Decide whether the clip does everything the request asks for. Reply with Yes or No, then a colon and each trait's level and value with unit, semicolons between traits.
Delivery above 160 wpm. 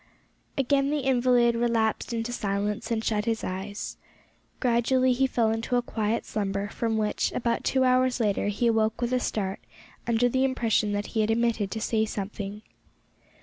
Yes: average, 170 wpm